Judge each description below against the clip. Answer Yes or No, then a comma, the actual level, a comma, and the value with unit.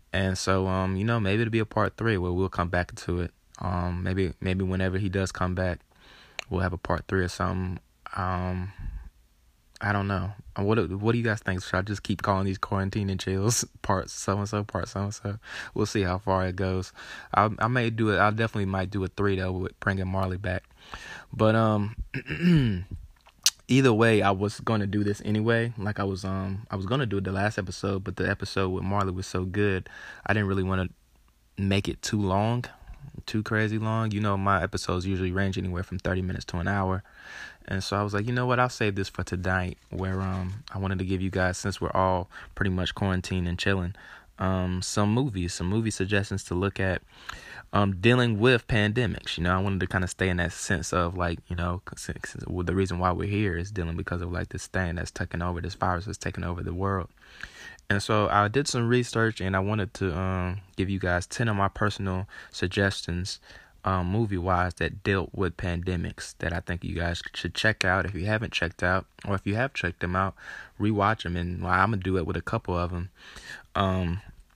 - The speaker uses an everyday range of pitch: No, narrow, 2.3 semitones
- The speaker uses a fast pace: Yes, fast, 225 wpm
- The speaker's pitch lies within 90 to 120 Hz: Yes, very low, 95 Hz